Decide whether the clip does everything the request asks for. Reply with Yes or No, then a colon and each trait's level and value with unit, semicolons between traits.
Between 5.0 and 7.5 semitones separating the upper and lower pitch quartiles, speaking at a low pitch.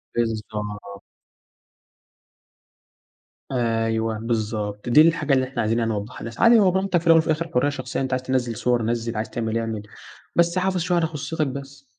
Yes: wide, 5.6 semitones; low, 125 Hz